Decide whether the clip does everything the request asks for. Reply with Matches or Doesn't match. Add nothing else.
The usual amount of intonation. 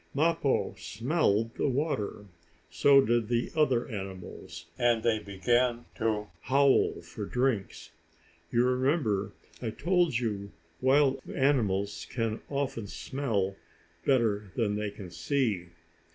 Matches